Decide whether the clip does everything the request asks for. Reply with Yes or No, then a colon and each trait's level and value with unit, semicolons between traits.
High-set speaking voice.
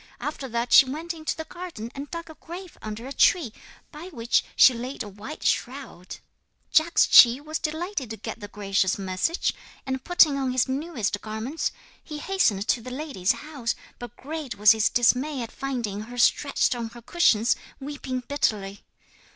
Yes: very high, 260 Hz